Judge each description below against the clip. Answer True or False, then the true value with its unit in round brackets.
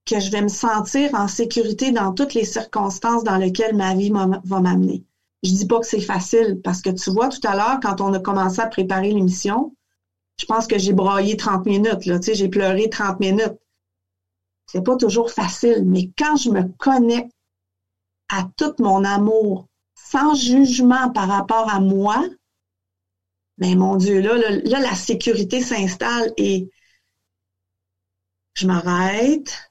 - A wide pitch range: False (3.7 semitones)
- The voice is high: True (200 Hz)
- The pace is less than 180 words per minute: True (170 wpm)